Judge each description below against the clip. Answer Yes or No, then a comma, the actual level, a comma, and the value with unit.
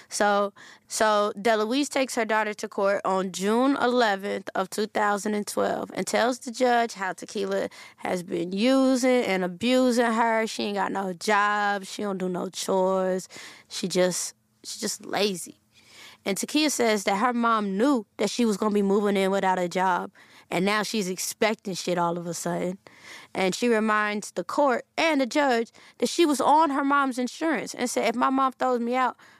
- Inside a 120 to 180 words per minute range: No, average, 190 wpm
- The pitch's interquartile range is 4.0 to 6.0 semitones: Yes, average, 4.3 semitones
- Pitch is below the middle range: No, high, 215 Hz